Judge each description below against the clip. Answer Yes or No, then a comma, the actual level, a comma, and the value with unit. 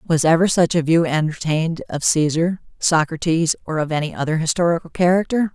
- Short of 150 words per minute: No, average, 160 wpm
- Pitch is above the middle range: No, medium, 165 Hz